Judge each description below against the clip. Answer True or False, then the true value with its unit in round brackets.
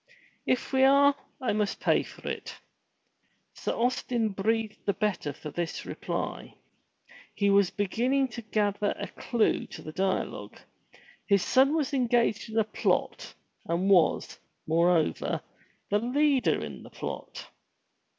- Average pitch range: True (4.5 semitones)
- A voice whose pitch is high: True (215 Hz)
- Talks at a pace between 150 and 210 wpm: False (140 wpm)